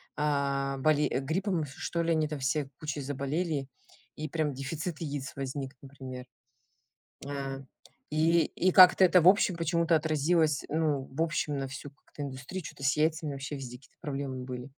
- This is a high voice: No, medium, 145 Hz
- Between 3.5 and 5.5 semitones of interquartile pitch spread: No, average, 2.8 semitones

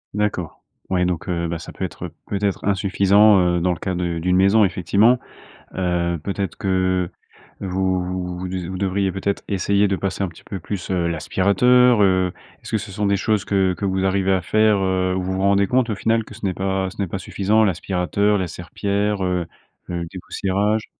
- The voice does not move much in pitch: Yes, narrow, 1.7 semitones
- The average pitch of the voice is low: Yes, very low, 95 Hz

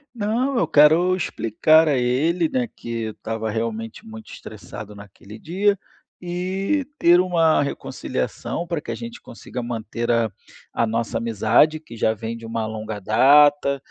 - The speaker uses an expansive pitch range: Yes, wide, 7.6 semitones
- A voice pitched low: Yes, low, 130 Hz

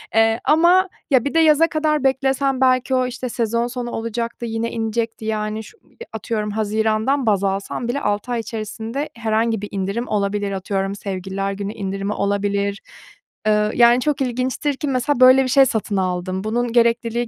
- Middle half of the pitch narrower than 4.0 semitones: Yes, average, 3.6 semitones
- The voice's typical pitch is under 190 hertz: No, high, 230 Hz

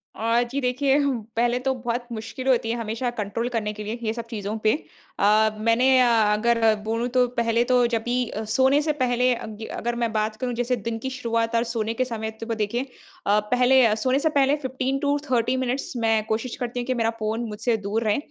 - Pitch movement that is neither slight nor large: No, narrow, 2.2 semitones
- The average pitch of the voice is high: Yes, high, 235 Hz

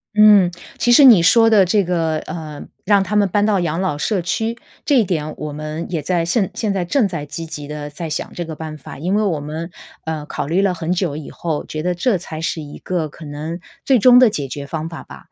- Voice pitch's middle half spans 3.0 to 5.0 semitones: Yes, average, 4.5 semitones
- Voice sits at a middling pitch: Yes, medium, 170 Hz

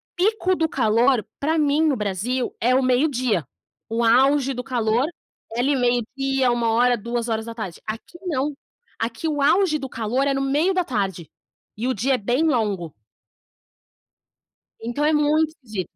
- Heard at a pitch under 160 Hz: No, very high, 250 Hz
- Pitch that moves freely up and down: No, average, 4.2 semitones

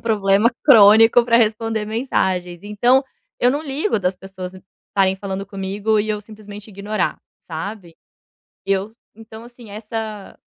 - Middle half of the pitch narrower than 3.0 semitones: Yes, narrow, 2.5 semitones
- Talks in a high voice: Yes, high, 210 Hz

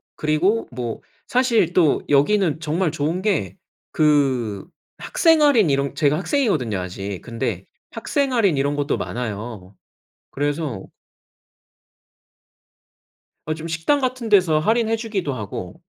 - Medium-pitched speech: Yes, medium, 155 Hz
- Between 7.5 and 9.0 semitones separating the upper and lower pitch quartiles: Yes, wide, 8.6 semitones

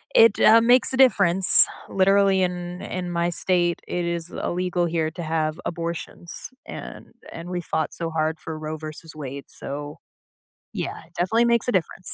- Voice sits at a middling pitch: Yes, medium, 175 Hz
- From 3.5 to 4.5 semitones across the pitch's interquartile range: No, average, 2.8 semitones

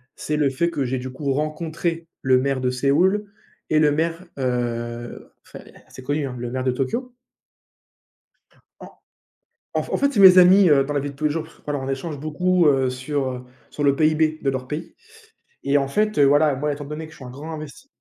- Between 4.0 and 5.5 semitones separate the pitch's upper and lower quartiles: No, average, 3.3 semitones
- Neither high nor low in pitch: Yes, medium, 145 Hz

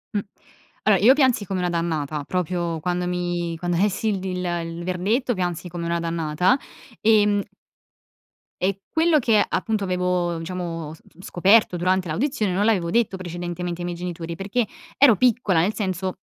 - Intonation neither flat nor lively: Yes, average, 3.1 semitones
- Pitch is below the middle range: No, medium, 180 Hz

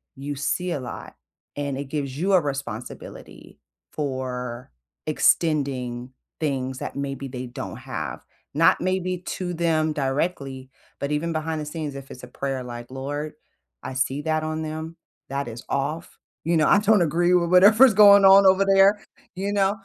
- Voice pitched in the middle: Yes, medium, 150 Hz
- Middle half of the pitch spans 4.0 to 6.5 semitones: Yes, average, 4.8 semitones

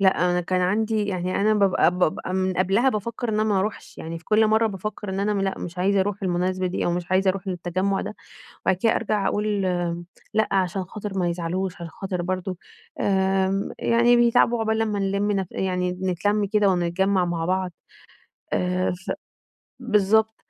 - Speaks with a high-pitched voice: Yes, high, 195 Hz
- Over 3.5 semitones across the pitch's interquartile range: No, narrow, 2.5 semitones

